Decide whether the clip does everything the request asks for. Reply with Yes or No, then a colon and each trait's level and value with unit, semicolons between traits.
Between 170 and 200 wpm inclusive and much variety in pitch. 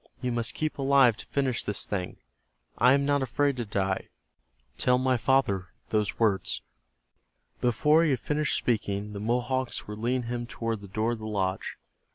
No: average, 175 wpm; average, 4.0 semitones